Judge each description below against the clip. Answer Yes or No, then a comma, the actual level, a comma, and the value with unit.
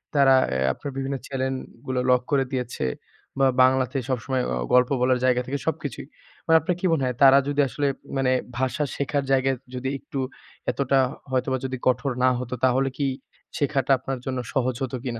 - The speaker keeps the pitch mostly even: Yes, narrow, 1.4 semitones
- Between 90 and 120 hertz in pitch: No, low, 130 Hz